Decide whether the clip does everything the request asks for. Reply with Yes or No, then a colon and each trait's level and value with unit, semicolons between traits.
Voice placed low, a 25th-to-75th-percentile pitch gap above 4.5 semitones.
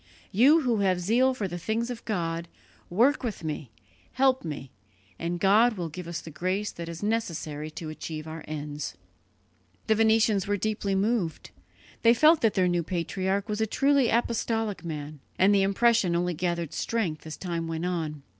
No: high, 190 Hz; average, 5.2 semitones